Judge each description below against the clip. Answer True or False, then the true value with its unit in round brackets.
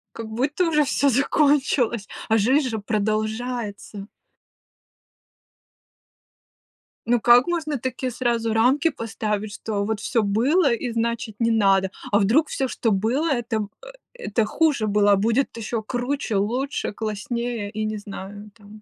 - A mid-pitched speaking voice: False (230 Hz)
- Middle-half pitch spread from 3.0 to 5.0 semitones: True (3.5 semitones)